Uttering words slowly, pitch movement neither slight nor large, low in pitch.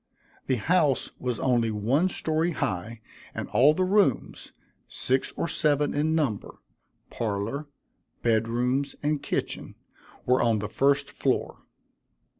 Yes: slow, 125 wpm; average, 4.9 semitones; low, 130 Hz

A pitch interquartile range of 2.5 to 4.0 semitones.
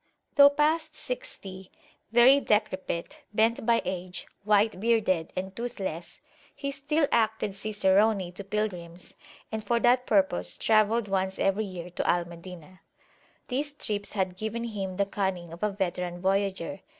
Yes: average, 3.7 semitones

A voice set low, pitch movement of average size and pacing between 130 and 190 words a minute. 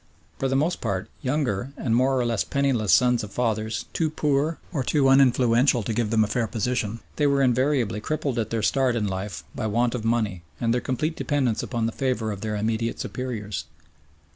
No: low, 120 Hz; average, 3.5 semitones; average, 200 wpm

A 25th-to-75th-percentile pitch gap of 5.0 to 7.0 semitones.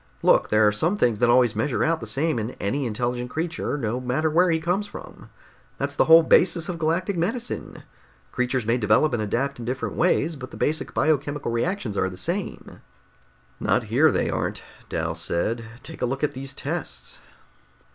Yes: wide, 5.6 semitones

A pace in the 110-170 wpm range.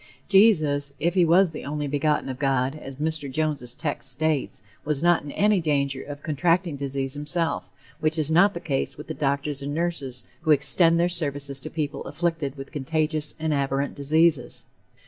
No: average, 180 wpm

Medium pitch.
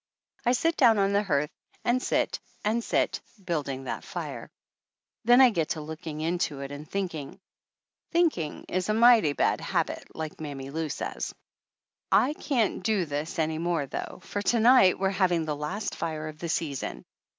Yes: medium, 170 Hz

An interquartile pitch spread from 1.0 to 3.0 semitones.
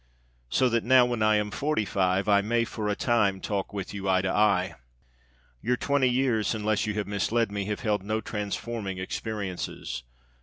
Yes: average, 2.7 semitones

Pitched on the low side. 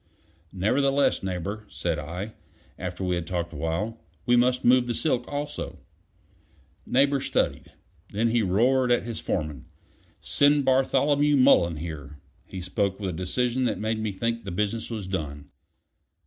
Yes: low, 110 Hz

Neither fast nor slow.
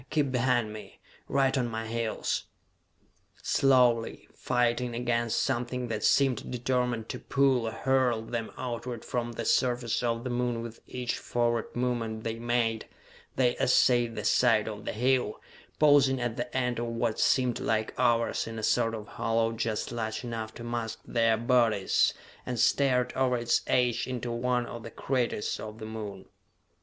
Yes: average, 165 wpm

